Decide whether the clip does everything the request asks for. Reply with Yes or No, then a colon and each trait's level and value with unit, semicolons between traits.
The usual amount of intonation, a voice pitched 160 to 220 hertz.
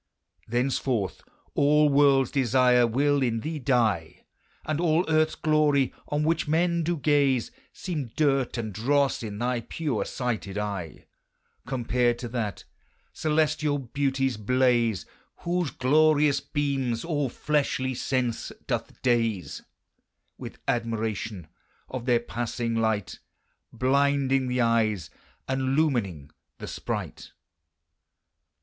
No: average, 3.9 semitones; low, 130 Hz